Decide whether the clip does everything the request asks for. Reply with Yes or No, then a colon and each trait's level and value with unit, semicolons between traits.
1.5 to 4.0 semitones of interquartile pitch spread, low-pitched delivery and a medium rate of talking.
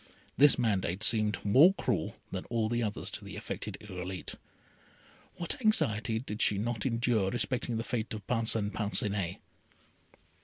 Yes: average, 2.7 semitones; low, 110 Hz; average, 145 wpm